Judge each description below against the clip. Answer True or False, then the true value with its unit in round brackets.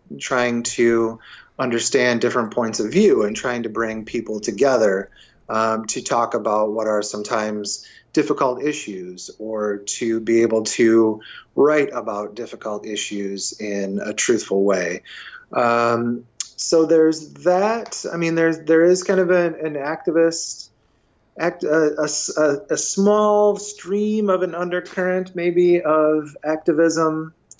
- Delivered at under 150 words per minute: True (135 wpm)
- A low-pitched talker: True (125 Hz)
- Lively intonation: True (7.1 semitones)